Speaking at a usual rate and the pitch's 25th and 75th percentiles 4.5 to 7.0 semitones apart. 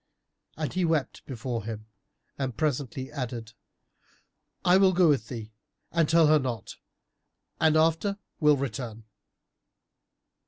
No: slow, 120 wpm; average, 5.3 semitones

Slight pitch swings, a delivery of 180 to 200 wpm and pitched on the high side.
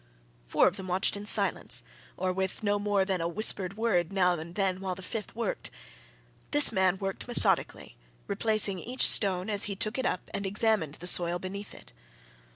Yes: narrow, 2.3 semitones; average, 185 wpm; high, 195 Hz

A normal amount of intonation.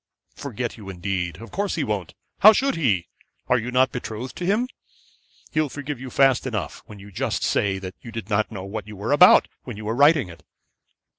No: wide, 5.7 semitones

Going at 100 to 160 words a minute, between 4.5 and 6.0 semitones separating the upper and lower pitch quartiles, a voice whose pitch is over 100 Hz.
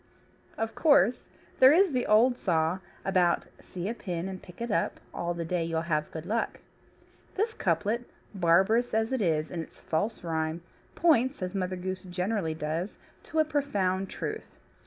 No: average, 170 wpm; wide, 5.5 semitones; medium, 185 Hz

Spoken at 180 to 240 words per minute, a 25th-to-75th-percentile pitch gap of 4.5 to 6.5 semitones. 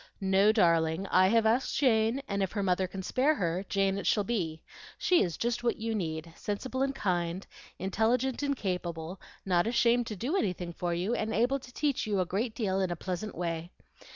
Yes: fast, 205 wpm; average, 4.9 semitones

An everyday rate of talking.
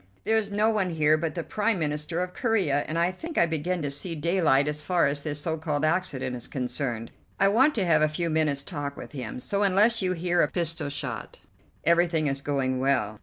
No: fast, 220 wpm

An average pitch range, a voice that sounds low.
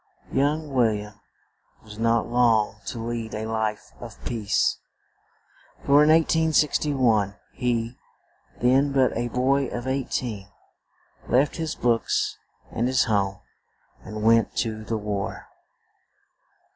Yes: average, 3.6 semitones; low, 120 Hz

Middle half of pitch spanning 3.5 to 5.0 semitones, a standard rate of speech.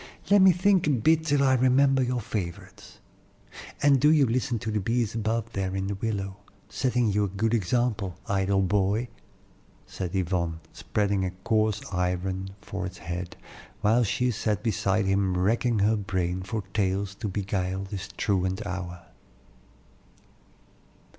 Yes: average, 3.8 semitones; average, 150 wpm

